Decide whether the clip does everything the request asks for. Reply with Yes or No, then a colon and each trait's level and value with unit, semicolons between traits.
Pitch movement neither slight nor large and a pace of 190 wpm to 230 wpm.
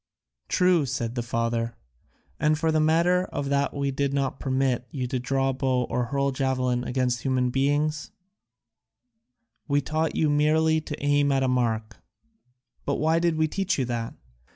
No: average, 3.4 semitones; average, 165 wpm